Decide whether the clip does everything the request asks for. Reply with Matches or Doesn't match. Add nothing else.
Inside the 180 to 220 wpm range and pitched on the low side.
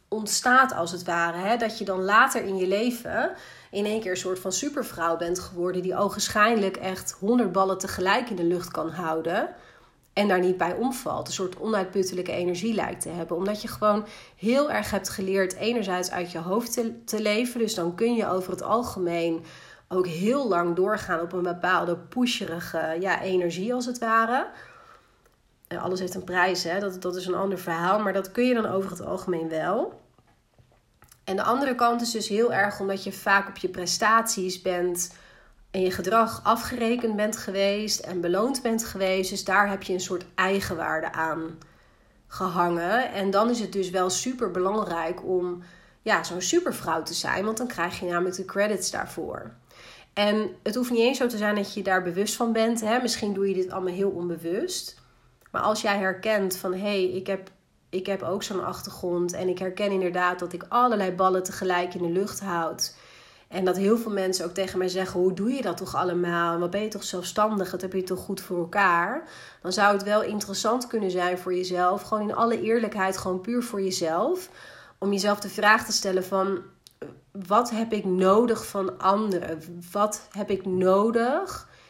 Doesn't match